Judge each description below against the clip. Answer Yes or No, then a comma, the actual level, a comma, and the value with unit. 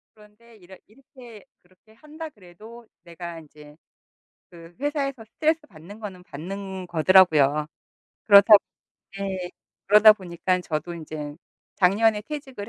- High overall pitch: Yes, high, 195 Hz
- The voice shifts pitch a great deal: No, average, 4.5 semitones